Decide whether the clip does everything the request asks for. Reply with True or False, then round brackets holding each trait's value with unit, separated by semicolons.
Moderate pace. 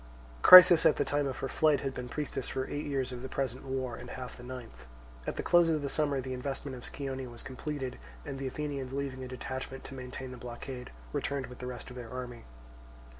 False (225 wpm)